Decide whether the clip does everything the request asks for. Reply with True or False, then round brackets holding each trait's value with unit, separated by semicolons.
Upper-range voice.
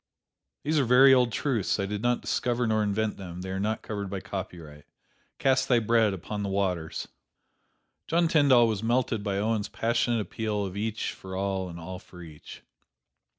False (105 Hz)